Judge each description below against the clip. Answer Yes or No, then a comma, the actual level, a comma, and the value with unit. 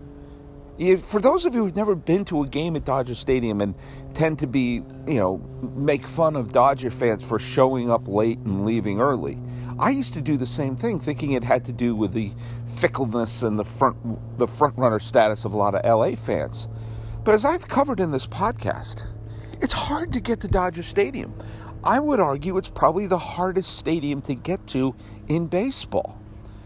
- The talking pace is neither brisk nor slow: Yes, average, 195 wpm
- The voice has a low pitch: Yes, low, 130 Hz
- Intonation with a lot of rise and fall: Yes, wide, 6.2 semitones